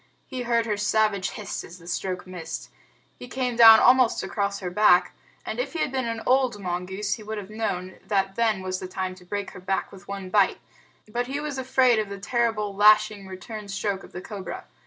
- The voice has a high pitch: Yes, high, 205 Hz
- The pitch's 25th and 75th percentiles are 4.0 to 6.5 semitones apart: No, average, 3.6 semitones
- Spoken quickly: Yes, fast, 215 wpm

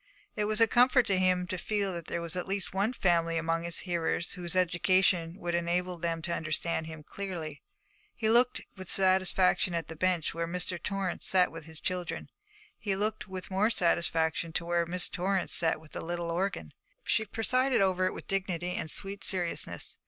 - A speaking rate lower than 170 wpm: No, average, 190 wpm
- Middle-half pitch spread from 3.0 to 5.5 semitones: No, narrow, 2.5 semitones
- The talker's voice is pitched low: No, medium, 180 Hz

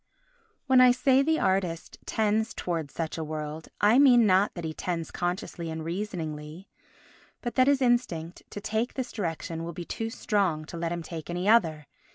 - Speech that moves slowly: No, average, 185 wpm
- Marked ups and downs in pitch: Yes, wide, 5.7 semitones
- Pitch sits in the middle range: Yes, medium, 180 Hz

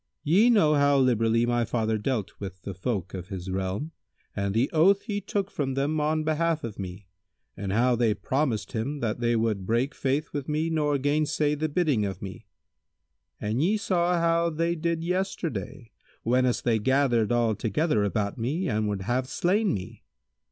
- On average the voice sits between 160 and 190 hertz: No, low, 130 Hz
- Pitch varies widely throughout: Yes, wide, 6.4 semitones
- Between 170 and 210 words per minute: Yes, average, 180 wpm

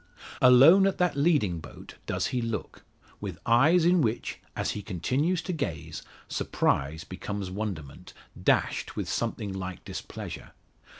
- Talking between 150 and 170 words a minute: No, slow, 135 wpm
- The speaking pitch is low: Yes, low, 115 Hz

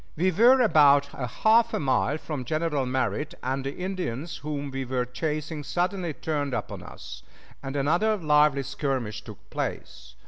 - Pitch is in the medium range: Yes, medium, 145 Hz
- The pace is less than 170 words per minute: Yes, average, 150 wpm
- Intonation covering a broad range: No, average, 4.0 semitones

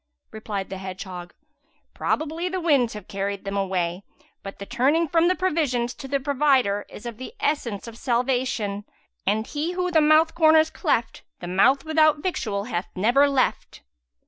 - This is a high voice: Yes, very high, 250 Hz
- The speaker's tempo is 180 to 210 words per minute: No, average, 165 wpm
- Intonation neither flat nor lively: No, wide, 7.6 semitones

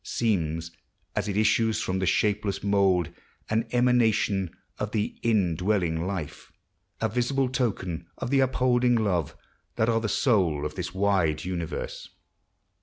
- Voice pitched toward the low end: Yes, low, 100 Hz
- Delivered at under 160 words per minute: Yes, slow, 135 wpm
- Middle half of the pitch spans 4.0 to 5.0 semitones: Yes, average, 4.5 semitones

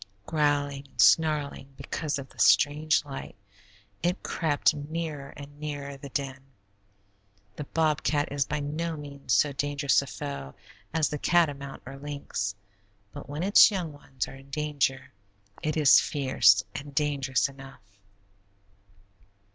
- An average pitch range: No, narrow, 1.6 semitones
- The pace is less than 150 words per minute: Yes, slow, 135 wpm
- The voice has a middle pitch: Yes, medium, 145 Hz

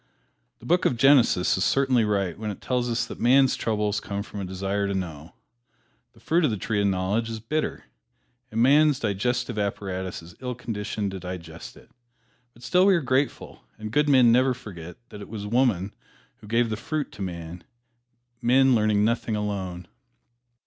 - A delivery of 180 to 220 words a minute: Yes, average, 185 wpm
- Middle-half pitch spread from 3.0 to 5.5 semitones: Yes, average, 4.4 semitones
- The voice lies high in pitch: No, low, 110 Hz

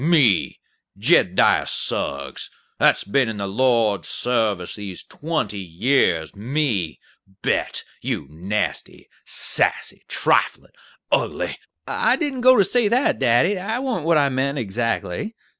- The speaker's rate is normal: No, slow, 130 wpm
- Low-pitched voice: Yes, low, 120 Hz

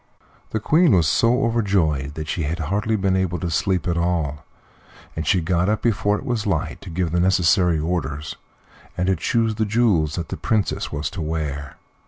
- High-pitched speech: No, very low, 90 Hz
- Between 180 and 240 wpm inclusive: Yes, average, 195 wpm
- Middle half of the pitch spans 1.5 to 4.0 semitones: No, average, 4.7 semitones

